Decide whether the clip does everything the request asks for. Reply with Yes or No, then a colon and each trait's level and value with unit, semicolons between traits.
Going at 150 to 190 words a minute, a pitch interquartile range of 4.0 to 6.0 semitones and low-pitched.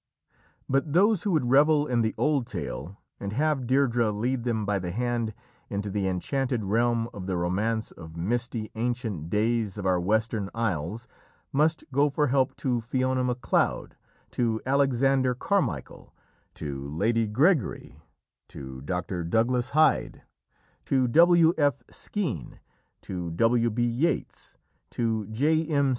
No: average, 140 wpm; average, 4.9 semitones; low, 120 Hz